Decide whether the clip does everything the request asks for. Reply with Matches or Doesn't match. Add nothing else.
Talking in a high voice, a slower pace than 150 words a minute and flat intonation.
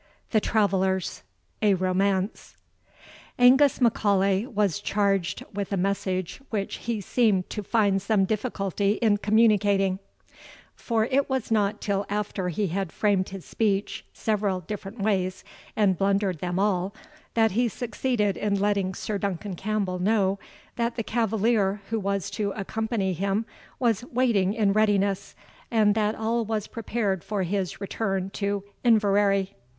Matches